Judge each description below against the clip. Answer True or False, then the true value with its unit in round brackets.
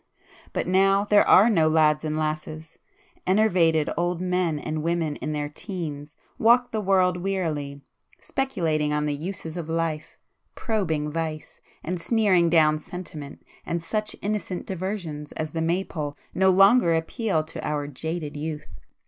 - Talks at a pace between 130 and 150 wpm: True (140 wpm)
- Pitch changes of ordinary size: True (3.7 semitones)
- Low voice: False (165 Hz)